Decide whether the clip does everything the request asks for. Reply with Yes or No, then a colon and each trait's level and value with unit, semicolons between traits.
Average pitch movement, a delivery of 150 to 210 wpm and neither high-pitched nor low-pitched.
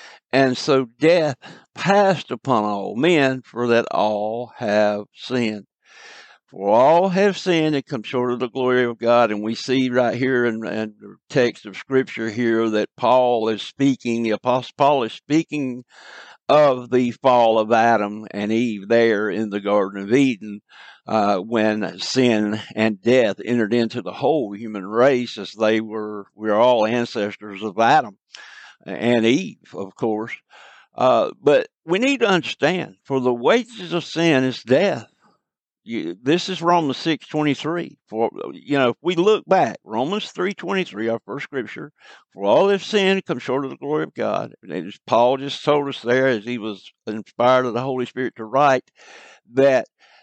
No: average, 4.1 semitones; average, 170 wpm; low, 125 Hz